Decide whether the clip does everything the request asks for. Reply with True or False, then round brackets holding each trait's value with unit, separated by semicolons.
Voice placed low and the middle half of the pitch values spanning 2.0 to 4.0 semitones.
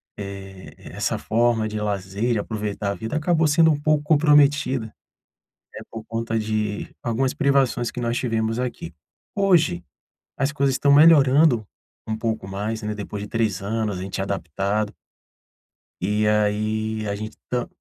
False (110 Hz; 4.5 semitones)